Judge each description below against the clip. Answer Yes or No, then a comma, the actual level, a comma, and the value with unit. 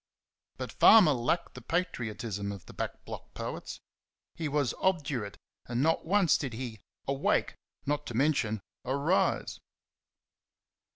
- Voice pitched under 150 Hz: Yes, low, 135 Hz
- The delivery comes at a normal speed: No, slow, 125 wpm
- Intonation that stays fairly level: No, average, 5.2 semitones